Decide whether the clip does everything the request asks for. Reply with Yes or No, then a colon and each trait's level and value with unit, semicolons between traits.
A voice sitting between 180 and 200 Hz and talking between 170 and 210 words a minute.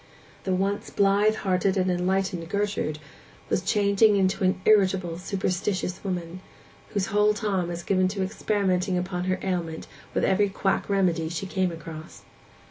No: high, 190 Hz; average, 145 wpm